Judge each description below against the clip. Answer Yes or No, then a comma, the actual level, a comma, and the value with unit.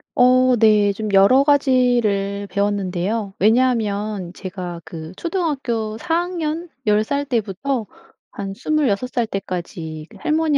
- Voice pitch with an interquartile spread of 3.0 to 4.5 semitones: No, average, 5.1 semitones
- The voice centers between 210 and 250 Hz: Yes, high, 220 Hz